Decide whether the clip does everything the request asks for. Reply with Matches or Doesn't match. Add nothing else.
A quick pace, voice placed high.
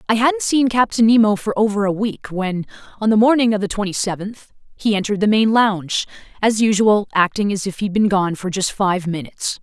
Matches